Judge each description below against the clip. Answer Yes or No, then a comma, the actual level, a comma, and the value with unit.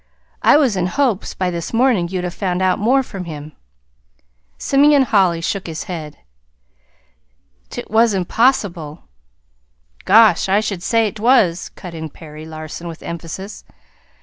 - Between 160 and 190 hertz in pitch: Yes, medium, 185 Hz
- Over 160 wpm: No, average, 145 wpm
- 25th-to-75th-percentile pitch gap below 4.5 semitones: No, average, 4.9 semitones